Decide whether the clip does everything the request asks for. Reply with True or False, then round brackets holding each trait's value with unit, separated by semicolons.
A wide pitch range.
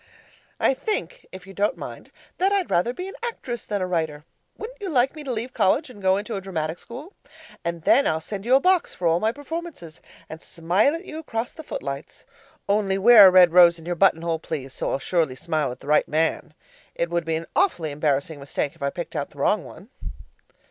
True (8.0 semitones)